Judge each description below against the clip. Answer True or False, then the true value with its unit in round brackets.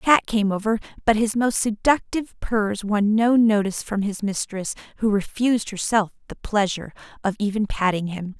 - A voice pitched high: True (210 Hz)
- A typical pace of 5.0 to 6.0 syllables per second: True (5.2 syllables/s)